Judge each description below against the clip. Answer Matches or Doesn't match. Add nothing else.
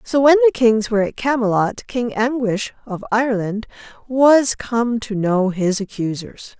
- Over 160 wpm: Doesn't match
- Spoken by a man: Doesn't match